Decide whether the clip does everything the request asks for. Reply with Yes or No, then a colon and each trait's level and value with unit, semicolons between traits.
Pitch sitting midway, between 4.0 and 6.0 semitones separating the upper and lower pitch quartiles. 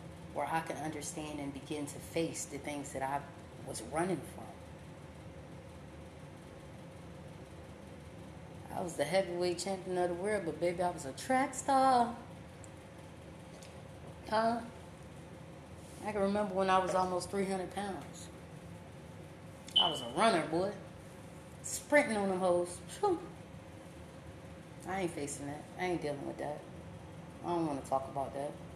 Yes: medium, 175 Hz; average, 4.8 semitones